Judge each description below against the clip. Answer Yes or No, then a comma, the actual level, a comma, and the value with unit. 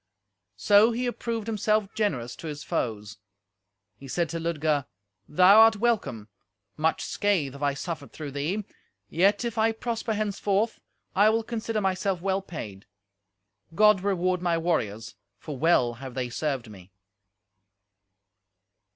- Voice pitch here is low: No, medium, 180 Hz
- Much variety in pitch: Yes, wide, 7.1 semitones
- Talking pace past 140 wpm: No, slow, 135 wpm